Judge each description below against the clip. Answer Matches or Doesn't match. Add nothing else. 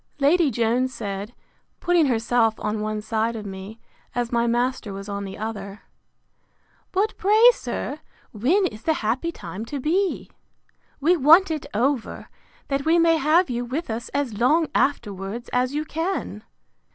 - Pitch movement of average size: Doesn't match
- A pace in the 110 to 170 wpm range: Matches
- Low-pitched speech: Doesn't match